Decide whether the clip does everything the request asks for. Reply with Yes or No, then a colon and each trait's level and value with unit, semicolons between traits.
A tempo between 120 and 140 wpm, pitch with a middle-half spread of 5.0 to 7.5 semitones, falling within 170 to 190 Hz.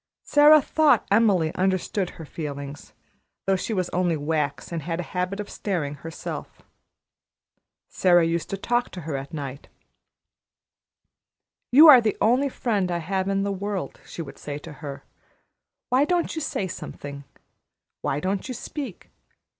No: average, 155 wpm; average, 5.3 semitones; medium, 185 Hz